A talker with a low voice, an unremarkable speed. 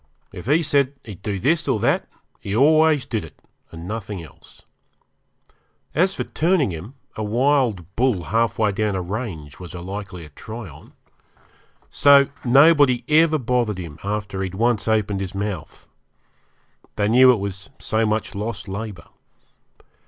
Yes: low, 110 Hz; average, 150 wpm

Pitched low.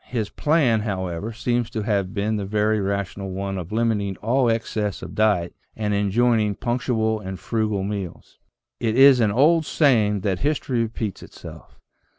Yes: low, 110 Hz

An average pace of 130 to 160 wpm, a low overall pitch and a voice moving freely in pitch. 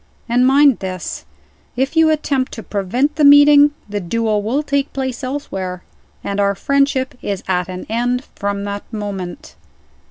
No: average, 155 wpm; high, 240 Hz; wide, 5.7 semitones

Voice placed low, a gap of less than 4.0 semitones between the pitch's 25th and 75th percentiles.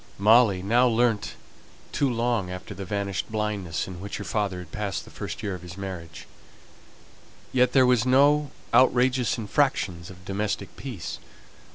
No: low, 105 Hz; average, 4.8 semitones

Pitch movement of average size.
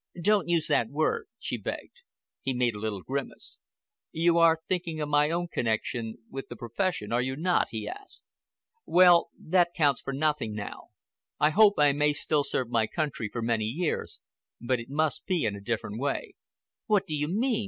No: wide, 6.4 semitones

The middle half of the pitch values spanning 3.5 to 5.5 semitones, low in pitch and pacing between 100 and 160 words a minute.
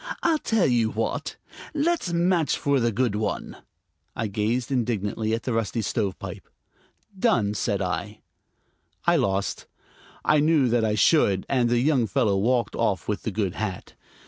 Yes: average, 5.0 semitones; low, 115 Hz; average, 155 wpm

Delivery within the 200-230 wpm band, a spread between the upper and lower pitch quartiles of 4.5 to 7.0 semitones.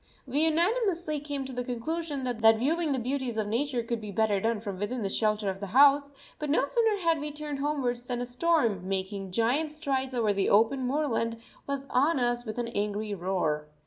Yes: fast, 205 wpm; average, 5.1 semitones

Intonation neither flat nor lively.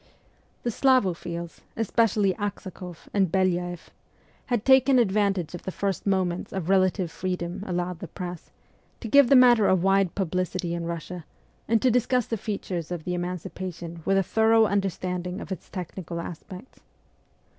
Yes: average, 3.0 semitones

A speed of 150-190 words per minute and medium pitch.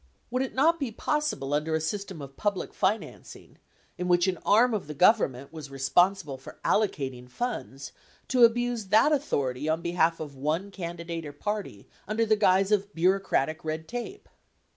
Yes: average, 175 wpm; medium, 180 Hz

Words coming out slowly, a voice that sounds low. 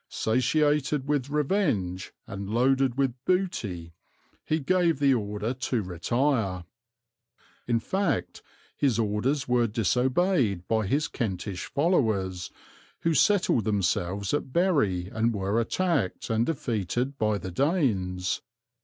Yes: slow, 115 wpm; low, 120 Hz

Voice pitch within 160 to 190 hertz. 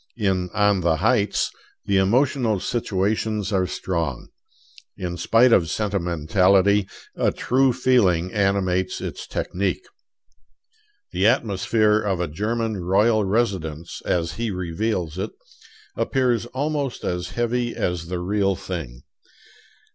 No: low, 100 Hz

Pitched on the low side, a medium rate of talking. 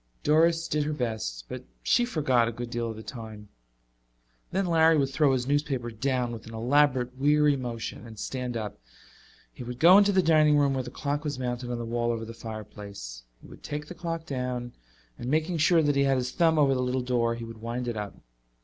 No: low, 125 Hz; fast, 220 wpm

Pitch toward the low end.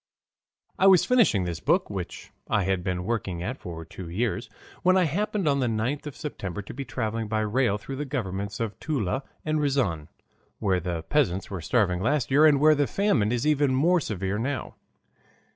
Yes: low, 115 Hz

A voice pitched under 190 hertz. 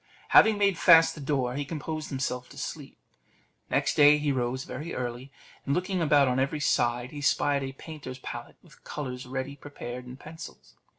Yes: medium, 140 Hz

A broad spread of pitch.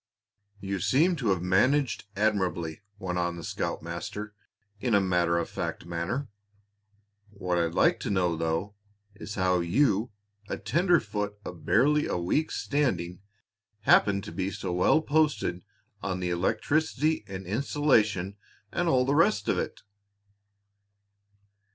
Yes: wide, 6.7 semitones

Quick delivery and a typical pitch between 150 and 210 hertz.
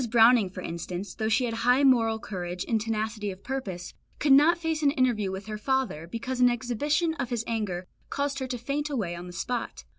No: fast, 210 wpm; high, 230 Hz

